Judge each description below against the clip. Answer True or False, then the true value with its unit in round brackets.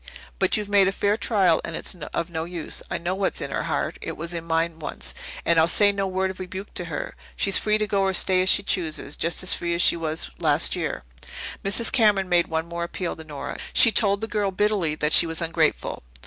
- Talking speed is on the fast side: True (240 wpm)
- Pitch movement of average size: True (3.3 semitones)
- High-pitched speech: False (180 Hz)